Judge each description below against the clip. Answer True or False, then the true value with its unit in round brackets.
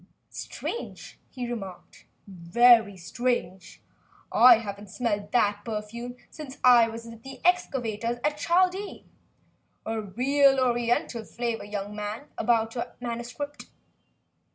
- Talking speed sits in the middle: False (110 wpm)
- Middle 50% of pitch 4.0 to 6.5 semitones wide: False (3.3 semitones)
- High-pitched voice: True (235 Hz)